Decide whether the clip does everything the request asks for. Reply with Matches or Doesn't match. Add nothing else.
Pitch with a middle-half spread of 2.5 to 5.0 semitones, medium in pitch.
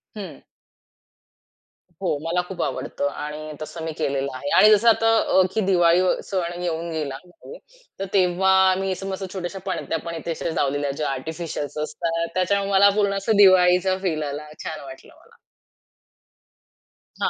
Matches